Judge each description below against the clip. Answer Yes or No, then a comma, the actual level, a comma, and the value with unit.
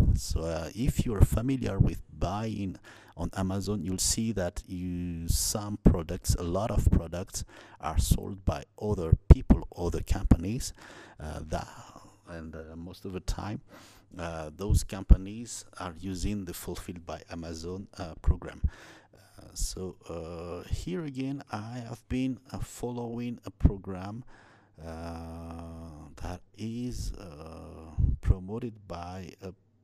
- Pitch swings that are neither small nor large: Yes, average, 3.8 semitones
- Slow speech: Yes, slow, 130 wpm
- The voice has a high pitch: No, very low, 95 Hz